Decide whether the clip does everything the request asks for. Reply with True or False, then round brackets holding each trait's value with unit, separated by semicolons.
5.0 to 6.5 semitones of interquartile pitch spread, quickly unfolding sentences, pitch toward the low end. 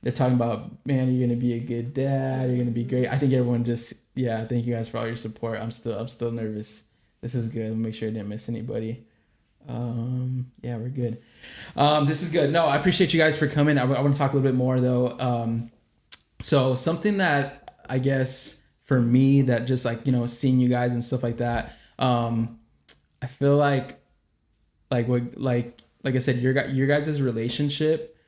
False (2.7 semitones; 215 wpm; 125 Hz)